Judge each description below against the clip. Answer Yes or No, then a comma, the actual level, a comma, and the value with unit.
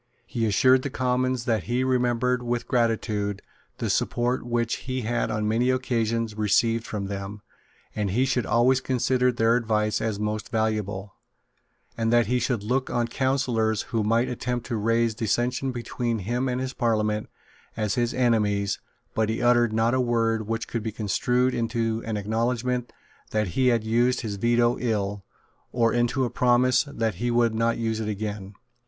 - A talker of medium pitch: No, low, 115 Hz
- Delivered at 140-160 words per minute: No, average, 170 wpm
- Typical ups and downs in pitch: No, narrow, 2.2 semitones